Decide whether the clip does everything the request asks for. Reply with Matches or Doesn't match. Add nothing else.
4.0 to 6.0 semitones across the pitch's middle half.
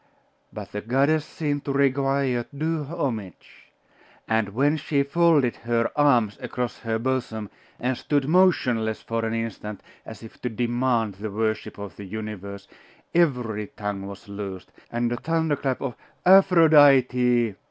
Matches